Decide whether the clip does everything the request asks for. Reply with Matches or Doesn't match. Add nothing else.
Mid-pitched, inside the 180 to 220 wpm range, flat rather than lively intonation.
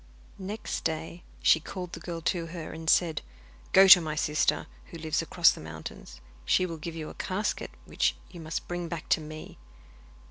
Matches